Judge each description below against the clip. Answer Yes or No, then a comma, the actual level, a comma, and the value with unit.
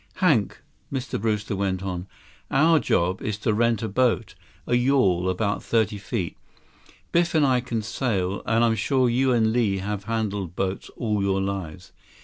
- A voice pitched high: No, low, 110 Hz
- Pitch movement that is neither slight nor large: Yes, average, 4.0 semitones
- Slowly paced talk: No, average, 165 wpm